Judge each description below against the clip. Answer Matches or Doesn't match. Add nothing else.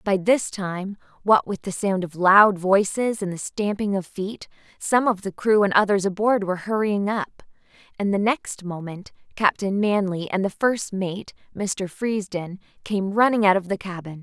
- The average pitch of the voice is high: Matches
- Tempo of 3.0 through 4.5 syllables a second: Matches